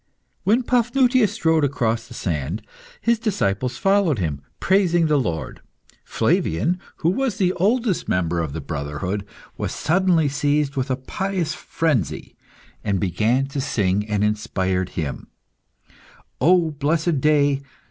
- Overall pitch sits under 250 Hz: Yes, medium, 140 Hz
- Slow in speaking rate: Yes, slow, 130 wpm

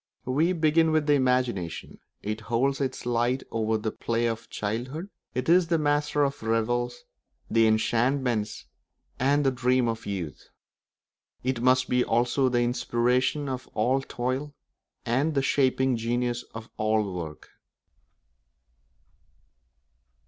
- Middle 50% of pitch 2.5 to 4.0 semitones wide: Yes, average, 3.2 semitones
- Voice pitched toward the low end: Yes, low, 125 Hz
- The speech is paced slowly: Yes, slow, 130 wpm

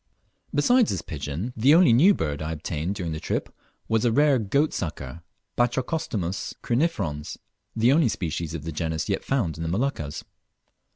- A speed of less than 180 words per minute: Yes, average, 165 wpm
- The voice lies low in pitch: Yes, low, 100 Hz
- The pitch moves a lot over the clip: Yes, wide, 9.0 semitones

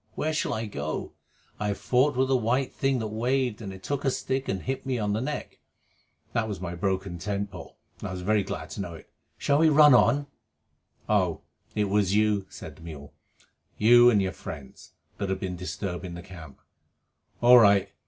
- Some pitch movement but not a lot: Yes, average, 5.0 semitones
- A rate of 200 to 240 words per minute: Yes, fast, 205 wpm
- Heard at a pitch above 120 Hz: No, low, 105 Hz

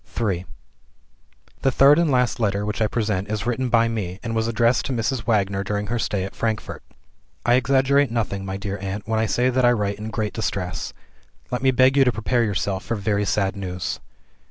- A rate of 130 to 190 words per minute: No, fast, 205 wpm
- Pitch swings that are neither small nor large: Yes, average, 3.4 semitones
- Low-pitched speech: Yes, low, 110 Hz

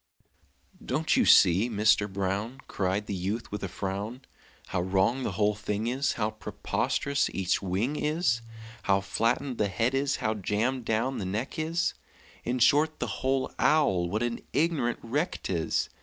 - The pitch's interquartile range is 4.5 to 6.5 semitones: Yes, average, 5.1 semitones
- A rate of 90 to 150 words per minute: No, average, 160 wpm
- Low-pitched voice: Yes, low, 110 Hz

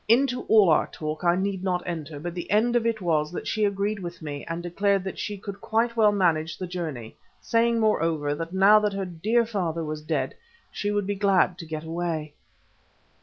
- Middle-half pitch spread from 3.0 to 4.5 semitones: Yes, average, 4.2 semitones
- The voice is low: No, medium, 185 Hz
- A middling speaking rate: No, fast, 210 wpm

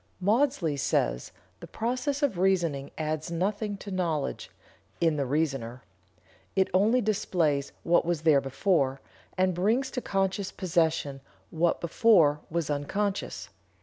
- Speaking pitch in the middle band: Yes, medium, 175 Hz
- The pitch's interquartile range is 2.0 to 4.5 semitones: No, average, 5.2 semitones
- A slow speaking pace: Yes, slow, 125 wpm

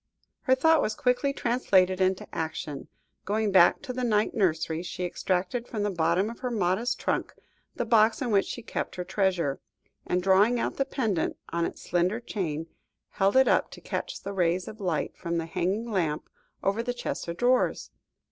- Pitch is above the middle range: Yes, high, 195 Hz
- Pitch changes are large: No, average, 4.9 semitones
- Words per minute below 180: No, average, 185 wpm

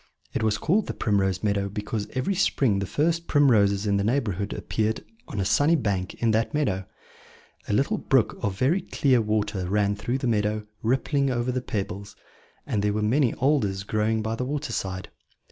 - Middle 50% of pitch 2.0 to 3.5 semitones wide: No, average, 4.4 semitones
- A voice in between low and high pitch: No, low, 110 Hz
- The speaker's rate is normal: Yes, average, 185 wpm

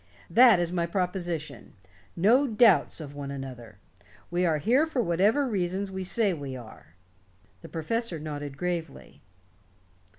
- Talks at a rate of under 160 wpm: Yes, slow, 135 wpm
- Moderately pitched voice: Yes, medium, 175 Hz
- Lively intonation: Yes, wide, 5.7 semitones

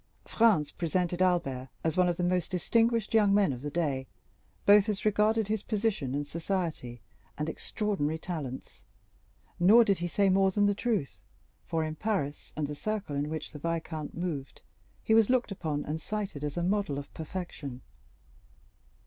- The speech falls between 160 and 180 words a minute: Yes, average, 170 wpm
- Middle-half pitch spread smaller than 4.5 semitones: No, wide, 5.4 semitones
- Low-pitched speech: No, medium, 175 Hz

